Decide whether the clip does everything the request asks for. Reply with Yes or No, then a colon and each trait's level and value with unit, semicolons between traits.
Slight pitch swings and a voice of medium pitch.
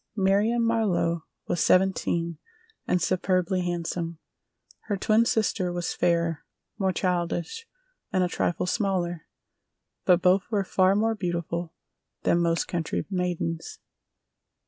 Yes: narrow, 2.3 semitones; medium, 180 Hz